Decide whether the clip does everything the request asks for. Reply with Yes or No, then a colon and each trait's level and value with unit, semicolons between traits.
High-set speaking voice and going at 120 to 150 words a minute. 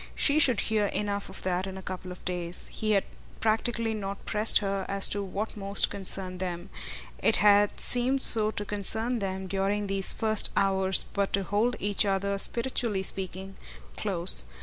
No: high, 200 Hz; average, 170 wpm